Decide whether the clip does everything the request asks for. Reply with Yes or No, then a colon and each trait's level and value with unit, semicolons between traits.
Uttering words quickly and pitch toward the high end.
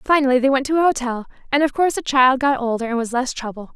Yes: fast, 270 wpm; very high, 260 Hz